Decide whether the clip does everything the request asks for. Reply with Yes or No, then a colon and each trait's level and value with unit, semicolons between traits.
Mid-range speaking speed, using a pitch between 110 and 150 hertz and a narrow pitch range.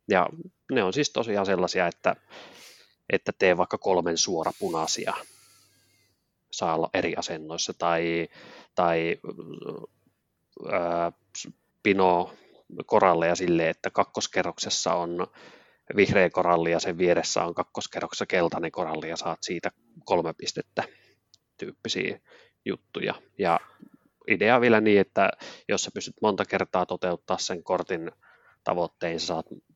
No: average, 120 wpm; very low, 85 Hz; narrow, 2.1 semitones